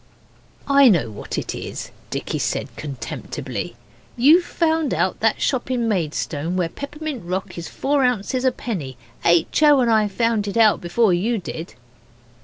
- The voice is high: Yes, high, 225 Hz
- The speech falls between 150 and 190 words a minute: Yes, average, 160 wpm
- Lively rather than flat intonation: Yes, wide, 7.2 semitones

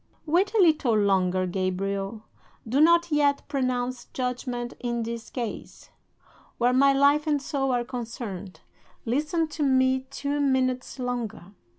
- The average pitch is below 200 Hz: No, very high, 255 Hz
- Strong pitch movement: No, average, 3.7 semitones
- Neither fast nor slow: No, slow, 130 wpm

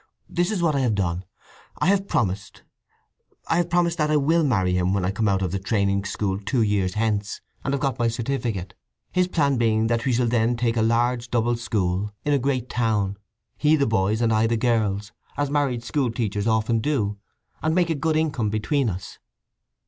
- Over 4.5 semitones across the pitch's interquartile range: Yes, average, 5.2 semitones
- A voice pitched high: No, low, 115 Hz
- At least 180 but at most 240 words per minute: Yes, average, 195 wpm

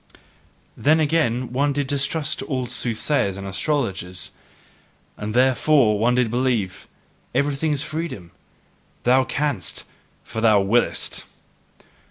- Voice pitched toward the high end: No, low, 130 Hz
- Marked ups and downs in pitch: No, average, 4.9 semitones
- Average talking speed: No, slow, 110 wpm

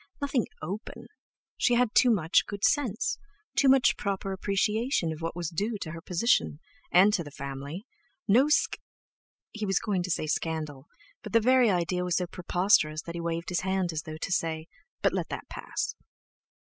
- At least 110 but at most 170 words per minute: No, average, 180 wpm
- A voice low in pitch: No, medium, 185 Hz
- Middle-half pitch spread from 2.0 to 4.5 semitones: No, average, 4.9 semitones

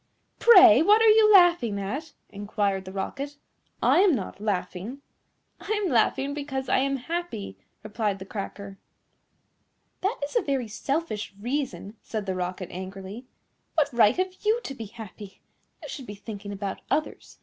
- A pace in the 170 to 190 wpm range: No, average, 160 wpm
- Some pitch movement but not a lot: No, wide, 7.4 semitones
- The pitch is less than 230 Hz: No, high, 235 Hz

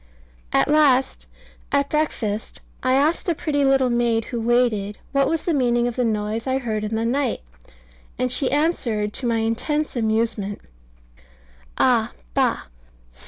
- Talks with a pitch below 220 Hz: No, high, 245 Hz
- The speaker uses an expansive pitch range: No, average, 3.8 semitones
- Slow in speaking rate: No, average, 150 wpm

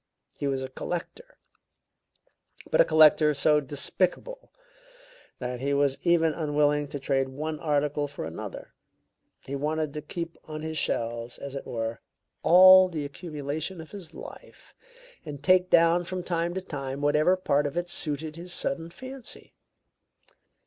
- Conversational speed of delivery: Yes, average, 150 wpm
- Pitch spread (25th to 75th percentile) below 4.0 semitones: Yes, average, 3.3 semitones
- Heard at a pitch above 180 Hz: No, medium, 155 Hz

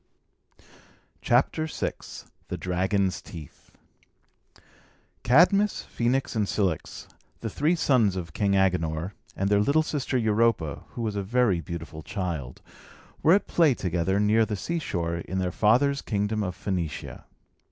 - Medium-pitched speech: No, low, 100 Hz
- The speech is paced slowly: Yes, slow, 130 wpm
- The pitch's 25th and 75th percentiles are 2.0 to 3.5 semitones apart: No, wide, 5.5 semitones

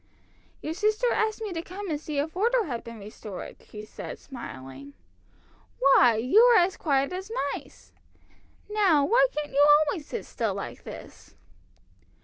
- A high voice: Yes, very high, 315 Hz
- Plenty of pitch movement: Yes, wide, 8.9 semitones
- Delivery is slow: No, average, 155 wpm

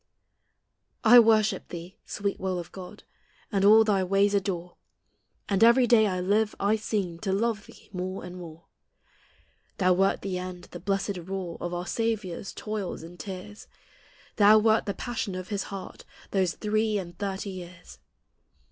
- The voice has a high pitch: Yes, high, 195 Hz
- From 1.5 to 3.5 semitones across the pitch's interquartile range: Yes, average, 2.7 semitones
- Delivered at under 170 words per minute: Yes, average, 160 wpm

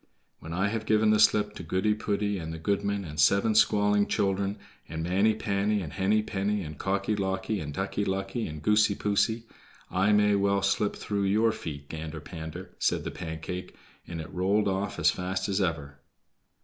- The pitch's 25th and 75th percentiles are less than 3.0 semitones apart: Yes, narrow, 2.5 semitones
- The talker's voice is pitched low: Yes, low, 100 Hz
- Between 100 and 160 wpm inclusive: No, average, 185 wpm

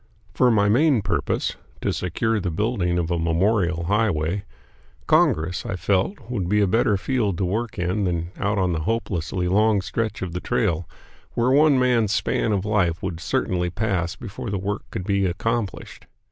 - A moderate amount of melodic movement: Yes, average, 4.0 semitones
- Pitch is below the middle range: Yes, low, 100 Hz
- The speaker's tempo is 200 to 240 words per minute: No, average, 175 wpm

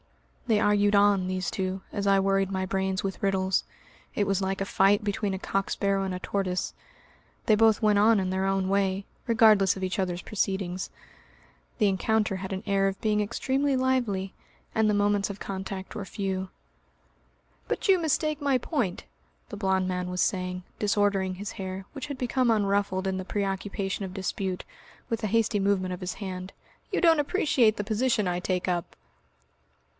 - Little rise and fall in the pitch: Yes, narrow, 2.1 semitones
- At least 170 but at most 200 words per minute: Yes, average, 180 wpm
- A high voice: Yes, high, 195 Hz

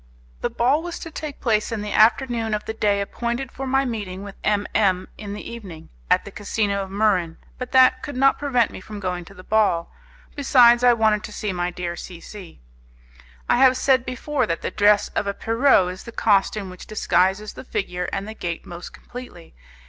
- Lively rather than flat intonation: No, average, 4.4 semitones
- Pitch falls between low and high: No, high, 215 Hz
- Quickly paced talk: Yes, fast, 210 wpm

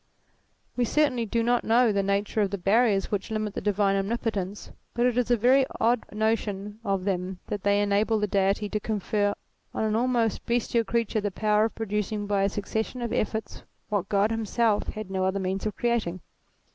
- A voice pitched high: Yes, high, 210 Hz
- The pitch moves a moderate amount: No, narrow, 2.3 semitones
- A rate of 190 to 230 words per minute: Yes, average, 195 wpm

